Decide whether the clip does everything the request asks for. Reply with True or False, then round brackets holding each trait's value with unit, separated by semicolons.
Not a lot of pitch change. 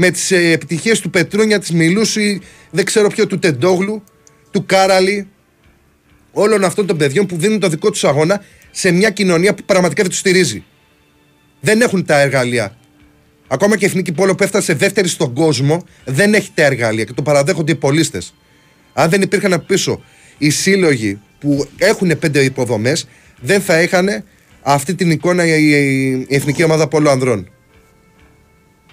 False (5.3 semitones)